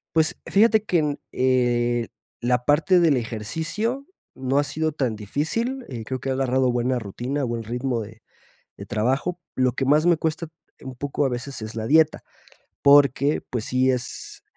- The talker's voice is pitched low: Yes, low, 130 Hz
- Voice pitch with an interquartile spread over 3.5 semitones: Yes, average, 4.3 semitones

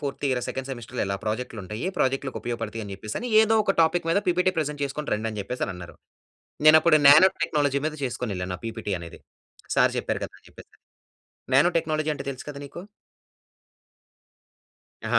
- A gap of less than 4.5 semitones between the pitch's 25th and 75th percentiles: No, wide, 5.6 semitones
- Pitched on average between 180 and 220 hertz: No, low, 135 Hz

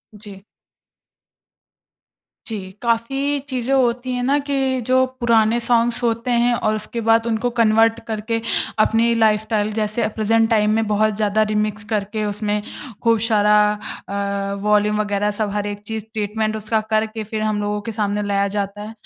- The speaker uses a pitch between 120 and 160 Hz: No, high, 220 Hz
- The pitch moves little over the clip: Yes, narrow, 1.7 semitones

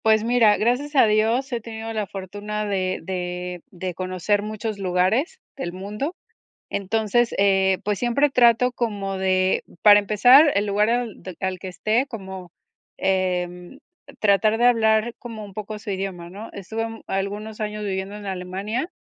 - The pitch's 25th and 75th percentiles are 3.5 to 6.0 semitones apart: No, average, 3.0 semitones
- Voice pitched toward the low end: No, high, 210 Hz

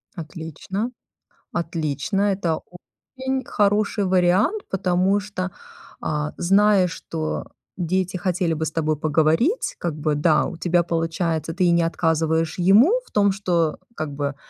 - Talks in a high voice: No, medium, 175 Hz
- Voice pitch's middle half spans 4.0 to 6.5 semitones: No, average, 3.4 semitones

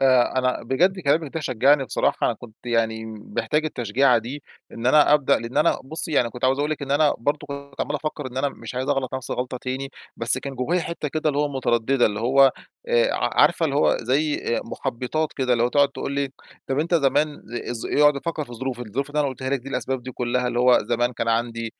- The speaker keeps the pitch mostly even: No, average, 3.2 semitones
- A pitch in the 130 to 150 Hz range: Yes, low, 135 Hz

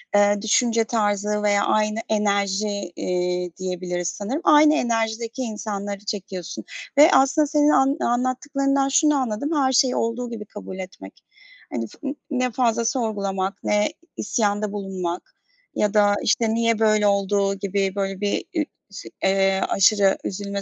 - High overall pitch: Yes, high, 210 Hz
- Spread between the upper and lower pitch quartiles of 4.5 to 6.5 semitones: No, average, 3.6 semitones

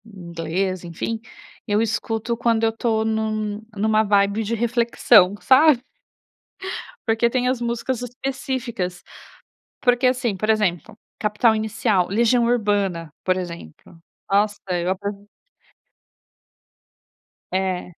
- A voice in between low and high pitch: No, high, 215 Hz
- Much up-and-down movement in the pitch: No, average, 3.6 semitones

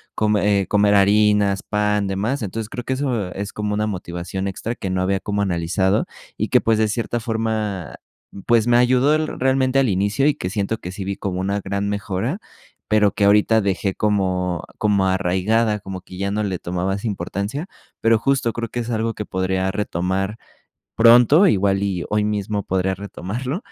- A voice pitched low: Yes, low, 105 Hz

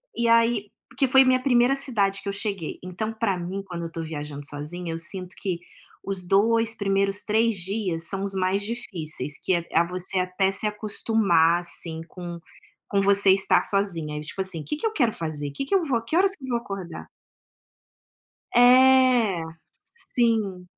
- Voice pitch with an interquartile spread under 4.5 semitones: No, average, 4.8 semitones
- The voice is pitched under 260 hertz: Yes, high, 195 Hz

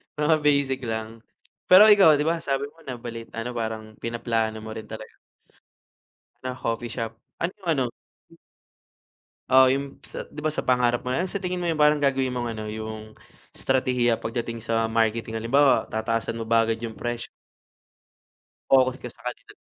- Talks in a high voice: No, low, 120 Hz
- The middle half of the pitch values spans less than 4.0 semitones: Yes, average, 3.3 semitones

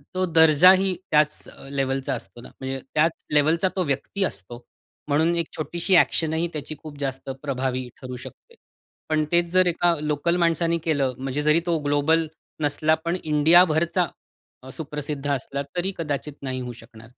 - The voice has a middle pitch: Yes, medium, 150 Hz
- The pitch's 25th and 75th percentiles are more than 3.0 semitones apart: Yes, average, 3.5 semitones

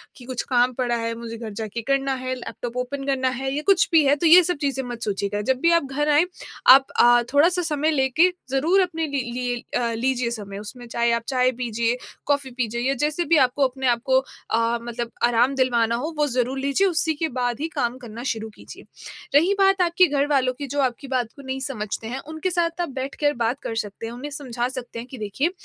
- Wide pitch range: No, average, 3.5 semitones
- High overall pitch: Yes, very high, 260 Hz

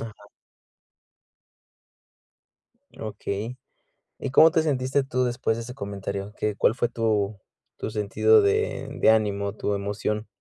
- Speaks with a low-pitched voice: Yes, low, 110 Hz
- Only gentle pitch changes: No, average, 3.9 semitones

